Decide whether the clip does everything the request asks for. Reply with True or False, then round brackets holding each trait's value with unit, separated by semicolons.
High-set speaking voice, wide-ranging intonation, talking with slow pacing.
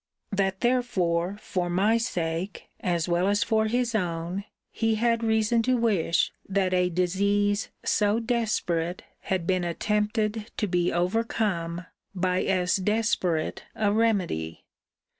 False (200 Hz; 3.8 semitones; 125 wpm)